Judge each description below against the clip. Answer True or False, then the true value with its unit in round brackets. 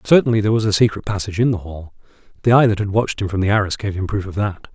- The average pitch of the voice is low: True (105 Hz)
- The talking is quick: True (290 wpm)